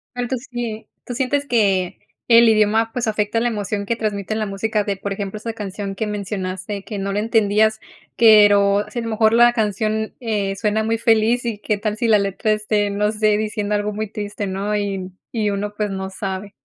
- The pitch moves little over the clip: Yes, narrow, 1.7 semitones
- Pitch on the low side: No, high, 210 Hz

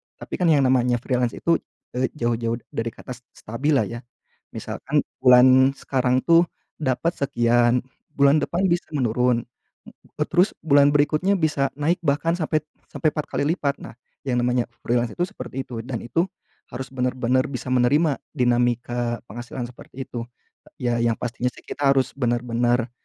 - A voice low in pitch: Yes, low, 130 Hz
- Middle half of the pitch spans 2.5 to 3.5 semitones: Yes, average, 3.2 semitones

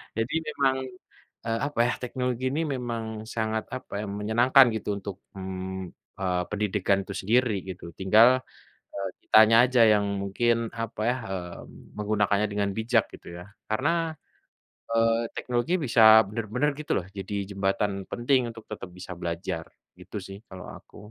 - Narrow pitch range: No, average, 3.6 semitones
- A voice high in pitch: No, low, 110 Hz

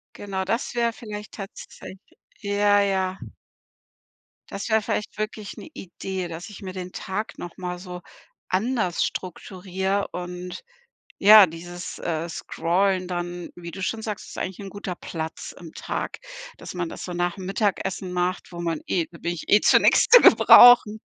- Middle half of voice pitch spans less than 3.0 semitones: Yes, narrow, 2.5 semitones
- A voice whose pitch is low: No, high, 190 Hz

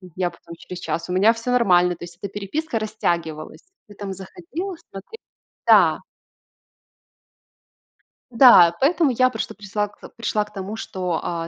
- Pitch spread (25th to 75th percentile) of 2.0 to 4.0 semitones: No, average, 4.7 semitones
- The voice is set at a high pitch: Yes, high, 200 Hz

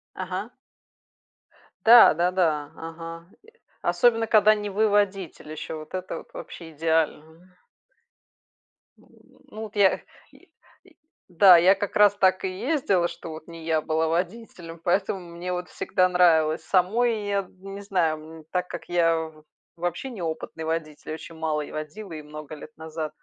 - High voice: No, medium, 175 Hz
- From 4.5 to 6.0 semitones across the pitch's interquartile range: No, average, 3.5 semitones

